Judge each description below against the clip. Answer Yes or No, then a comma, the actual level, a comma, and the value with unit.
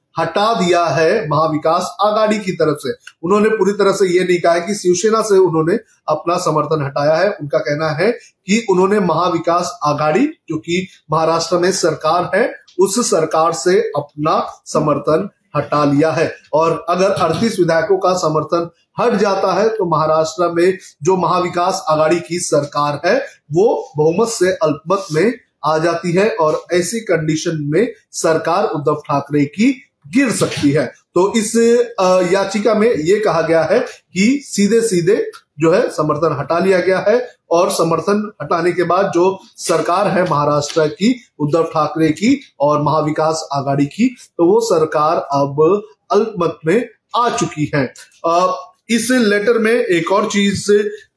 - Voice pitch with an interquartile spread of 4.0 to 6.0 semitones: Yes, average, 4.6 semitones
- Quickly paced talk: No, average, 155 wpm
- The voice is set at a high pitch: No, medium, 175 Hz